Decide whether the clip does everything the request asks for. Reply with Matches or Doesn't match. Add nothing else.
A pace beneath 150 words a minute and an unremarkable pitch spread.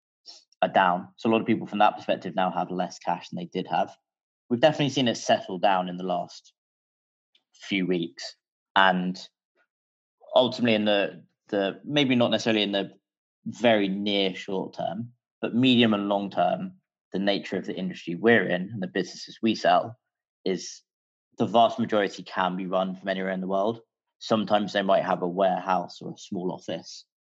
Doesn't match